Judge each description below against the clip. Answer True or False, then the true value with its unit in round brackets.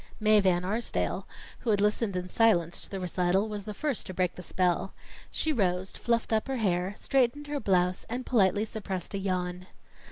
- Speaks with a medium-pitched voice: False (200 Hz)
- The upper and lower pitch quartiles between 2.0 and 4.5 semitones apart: True (3.7 semitones)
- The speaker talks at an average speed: True (190 wpm)